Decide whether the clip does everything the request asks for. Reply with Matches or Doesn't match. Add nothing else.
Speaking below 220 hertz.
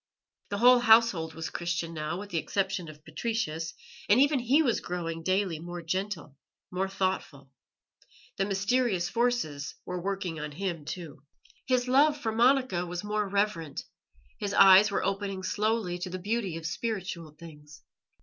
Matches